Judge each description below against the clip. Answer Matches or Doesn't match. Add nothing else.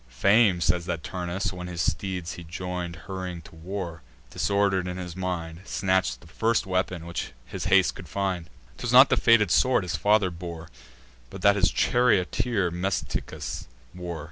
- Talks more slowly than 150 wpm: Doesn't match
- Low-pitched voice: Matches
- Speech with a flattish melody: Matches